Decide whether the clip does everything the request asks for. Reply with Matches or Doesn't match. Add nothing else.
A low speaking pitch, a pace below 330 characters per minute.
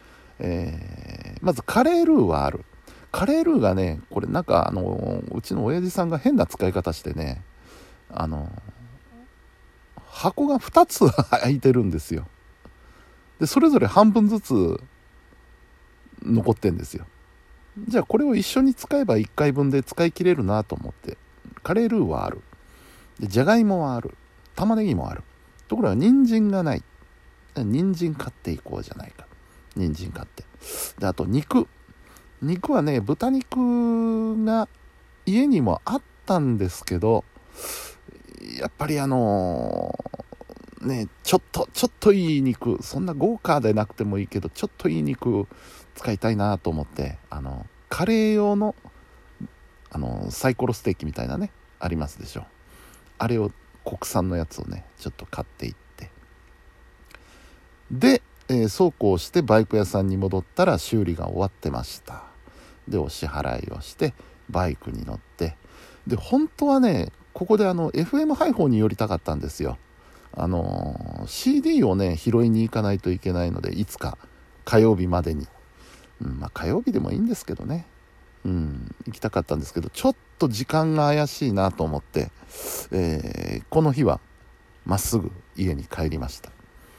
Matches